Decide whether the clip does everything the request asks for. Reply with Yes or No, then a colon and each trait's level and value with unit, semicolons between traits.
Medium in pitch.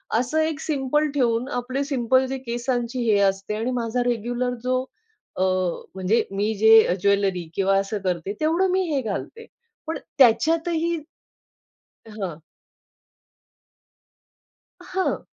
No: high, 245 Hz